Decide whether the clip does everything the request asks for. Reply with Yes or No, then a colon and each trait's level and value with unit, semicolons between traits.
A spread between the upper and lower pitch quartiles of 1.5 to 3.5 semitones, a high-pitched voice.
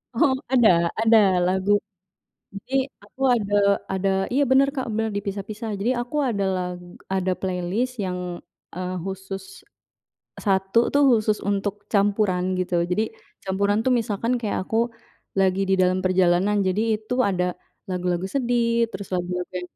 Yes: average, 3.1 semitones; high, 200 Hz